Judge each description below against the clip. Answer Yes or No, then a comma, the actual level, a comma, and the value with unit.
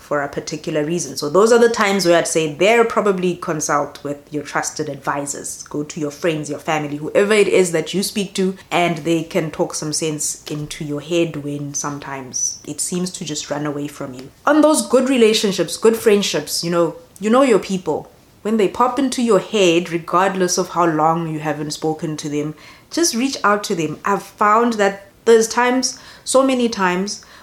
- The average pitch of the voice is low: No, medium, 170 Hz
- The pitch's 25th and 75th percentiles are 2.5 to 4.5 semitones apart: No, average, 5.2 semitones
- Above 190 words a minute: Yes, average, 200 wpm